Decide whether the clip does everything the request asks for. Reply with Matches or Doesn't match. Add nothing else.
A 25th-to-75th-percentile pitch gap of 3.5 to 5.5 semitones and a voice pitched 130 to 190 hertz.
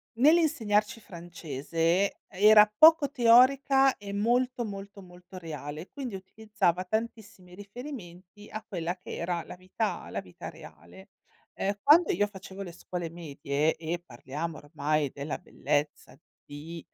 Matches